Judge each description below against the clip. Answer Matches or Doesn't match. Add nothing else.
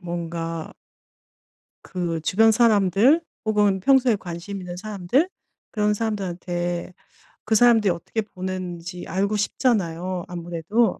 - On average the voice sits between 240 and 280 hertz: Doesn't match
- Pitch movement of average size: Matches